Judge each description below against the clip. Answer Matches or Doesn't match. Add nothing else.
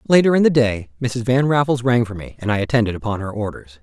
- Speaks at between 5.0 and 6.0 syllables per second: Doesn't match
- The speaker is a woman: Doesn't match